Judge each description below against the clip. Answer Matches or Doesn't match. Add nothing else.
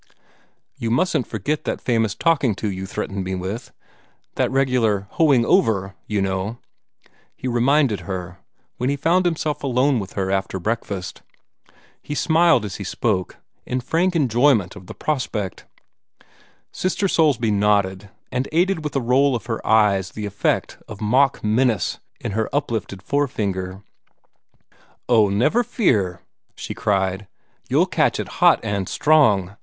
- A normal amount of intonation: Doesn't match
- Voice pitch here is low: Matches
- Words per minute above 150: Doesn't match